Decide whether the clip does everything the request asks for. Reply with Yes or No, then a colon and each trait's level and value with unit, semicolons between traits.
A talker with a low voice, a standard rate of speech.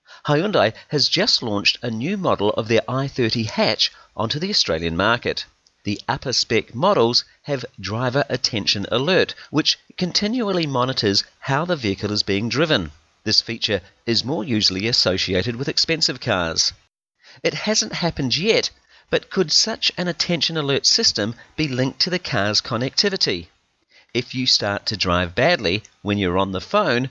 Yes: low, 125 Hz; average, 155 wpm